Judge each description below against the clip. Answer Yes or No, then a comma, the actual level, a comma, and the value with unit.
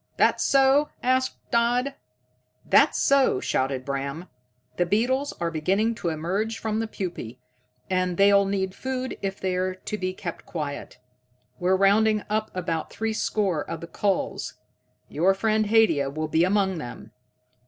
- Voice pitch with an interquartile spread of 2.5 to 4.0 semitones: No, average, 4.7 semitones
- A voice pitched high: Yes, high, 195 Hz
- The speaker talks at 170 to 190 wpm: No, average, 145 wpm